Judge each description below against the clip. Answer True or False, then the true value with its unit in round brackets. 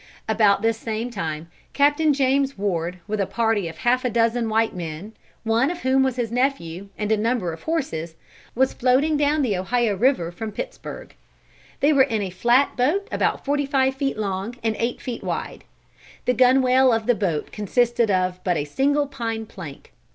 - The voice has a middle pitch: False (230 Hz)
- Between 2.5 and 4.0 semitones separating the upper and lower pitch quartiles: False (4.9 semitones)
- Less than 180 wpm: False (185 wpm)